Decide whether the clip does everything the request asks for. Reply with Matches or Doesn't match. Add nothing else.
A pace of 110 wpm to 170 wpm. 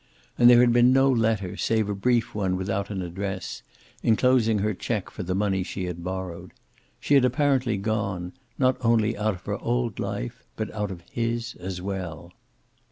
Doesn't match